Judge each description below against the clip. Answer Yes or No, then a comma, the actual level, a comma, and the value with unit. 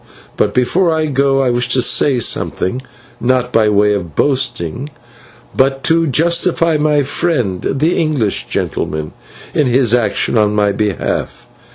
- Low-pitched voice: Yes, low, 130 Hz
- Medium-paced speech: Yes, average, 145 wpm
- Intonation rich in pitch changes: Yes, wide, 5.8 semitones